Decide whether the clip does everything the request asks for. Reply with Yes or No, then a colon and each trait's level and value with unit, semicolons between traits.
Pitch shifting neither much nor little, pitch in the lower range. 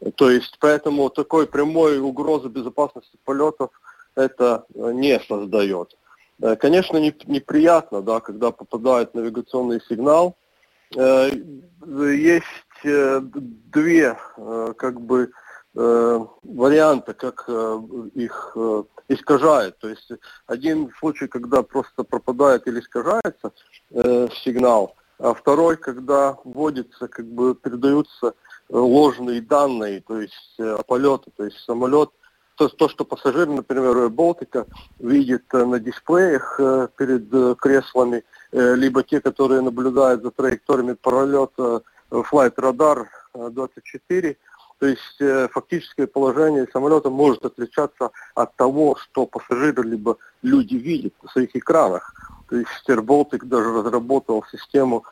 Yes: average, 3.1 semitones; low, 130 Hz